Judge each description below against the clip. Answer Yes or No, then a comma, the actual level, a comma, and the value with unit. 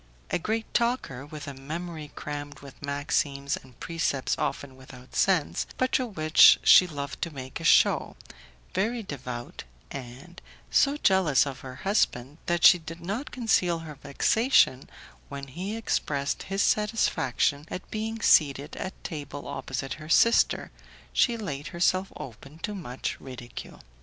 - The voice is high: No, medium, 155 Hz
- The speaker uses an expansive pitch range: Yes, wide, 5.7 semitones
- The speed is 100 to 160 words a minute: Yes, average, 145 wpm